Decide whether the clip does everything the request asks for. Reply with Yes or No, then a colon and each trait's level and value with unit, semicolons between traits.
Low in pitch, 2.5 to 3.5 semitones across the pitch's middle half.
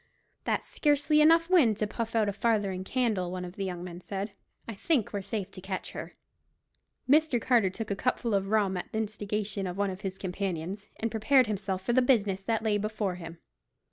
No: high, 205 Hz; average, 3.2 semitones